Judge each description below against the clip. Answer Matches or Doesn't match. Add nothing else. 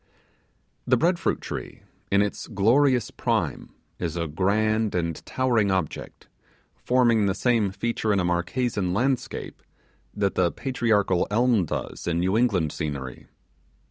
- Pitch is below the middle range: Matches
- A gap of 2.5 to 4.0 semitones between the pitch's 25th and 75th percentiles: Doesn't match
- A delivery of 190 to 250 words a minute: Doesn't match